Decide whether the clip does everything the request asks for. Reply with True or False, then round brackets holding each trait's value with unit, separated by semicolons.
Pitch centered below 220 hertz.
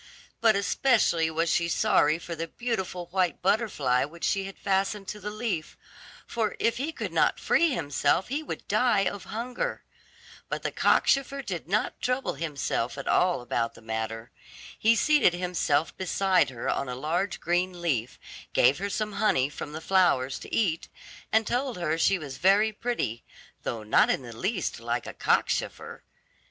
True (185 Hz)